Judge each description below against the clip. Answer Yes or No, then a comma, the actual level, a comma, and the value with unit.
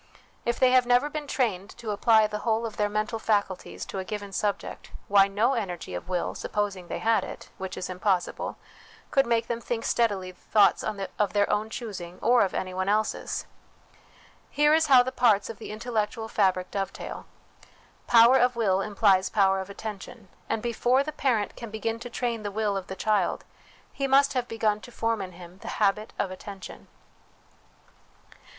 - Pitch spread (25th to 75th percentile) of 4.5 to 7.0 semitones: No, average, 3.3 semitones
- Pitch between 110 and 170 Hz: No, high, 215 Hz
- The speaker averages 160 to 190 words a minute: Yes, average, 180 wpm